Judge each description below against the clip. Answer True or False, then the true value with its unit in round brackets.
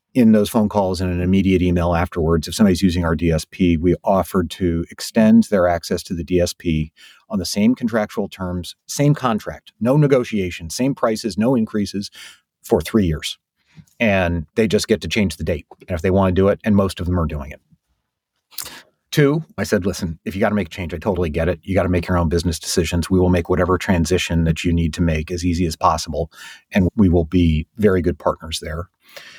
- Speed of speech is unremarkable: False (215 wpm)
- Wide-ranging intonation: False (3.1 semitones)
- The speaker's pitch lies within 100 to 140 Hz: False (90 Hz)